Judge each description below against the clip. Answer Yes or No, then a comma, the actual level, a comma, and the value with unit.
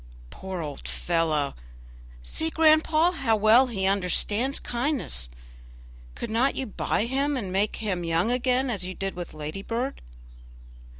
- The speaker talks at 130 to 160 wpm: Yes, slow, 135 wpm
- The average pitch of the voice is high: Yes, high, 215 Hz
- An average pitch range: No, wide, 6.5 semitones